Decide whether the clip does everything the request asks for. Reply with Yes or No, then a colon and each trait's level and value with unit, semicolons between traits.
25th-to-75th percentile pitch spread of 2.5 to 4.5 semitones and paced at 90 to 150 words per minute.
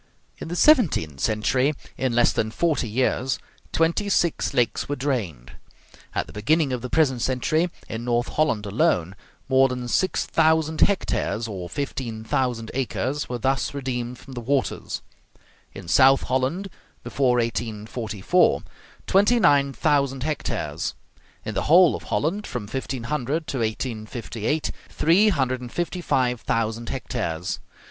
No: average, 4.9 semitones; average, 140 wpm